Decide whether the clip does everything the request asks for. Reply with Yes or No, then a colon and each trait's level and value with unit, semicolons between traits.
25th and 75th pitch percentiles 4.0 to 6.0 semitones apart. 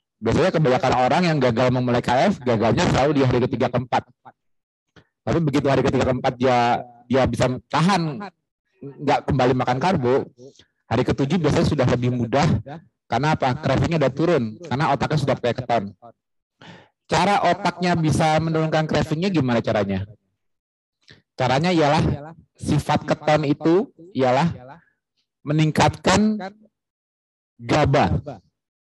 Yes: average, 4.5 semitones